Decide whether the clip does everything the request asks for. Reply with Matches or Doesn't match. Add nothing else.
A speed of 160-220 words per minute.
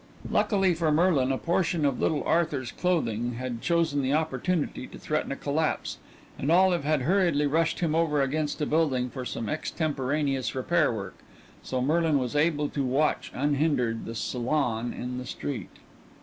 Matches